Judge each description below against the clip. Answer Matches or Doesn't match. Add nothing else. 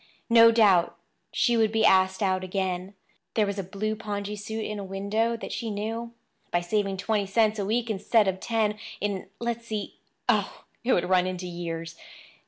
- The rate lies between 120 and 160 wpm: Doesn't match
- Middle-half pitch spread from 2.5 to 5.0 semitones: Matches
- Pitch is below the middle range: Doesn't match